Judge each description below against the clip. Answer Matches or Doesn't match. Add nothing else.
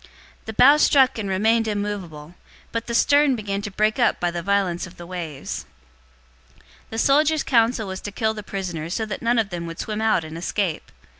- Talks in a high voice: Matches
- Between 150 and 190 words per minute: Doesn't match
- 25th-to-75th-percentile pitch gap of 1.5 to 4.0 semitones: Doesn't match